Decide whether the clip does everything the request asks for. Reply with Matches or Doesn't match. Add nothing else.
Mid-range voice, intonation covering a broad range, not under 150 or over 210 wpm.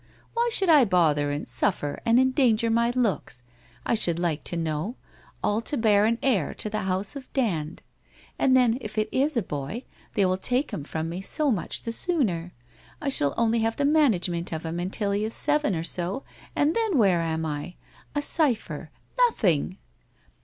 Doesn't match